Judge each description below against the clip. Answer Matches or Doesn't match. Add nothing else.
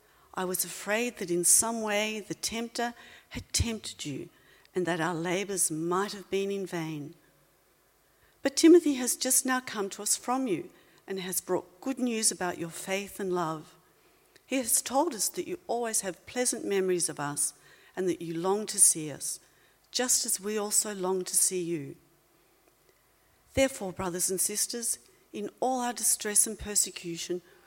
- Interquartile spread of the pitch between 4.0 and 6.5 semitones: Matches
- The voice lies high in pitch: Matches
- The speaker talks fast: Doesn't match